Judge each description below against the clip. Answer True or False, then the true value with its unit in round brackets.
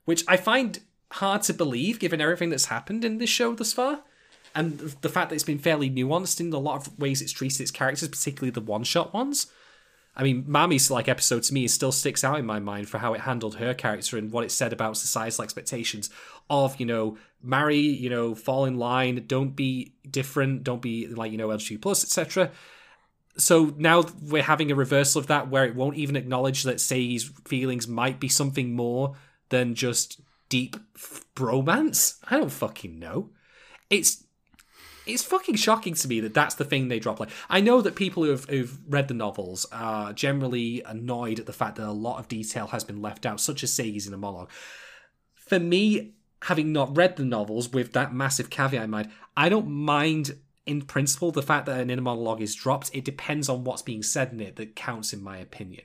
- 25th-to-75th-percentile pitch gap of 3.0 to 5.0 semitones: True (4.3 semitones)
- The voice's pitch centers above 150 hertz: False (135 Hz)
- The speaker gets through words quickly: True (210 wpm)